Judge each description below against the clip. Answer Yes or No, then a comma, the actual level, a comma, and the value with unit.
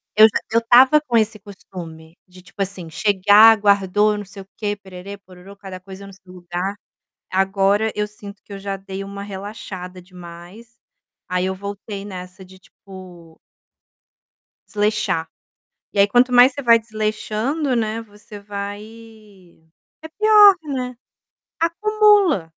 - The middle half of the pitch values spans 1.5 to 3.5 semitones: Yes, average, 2.8 semitones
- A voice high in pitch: Yes, high, 200 Hz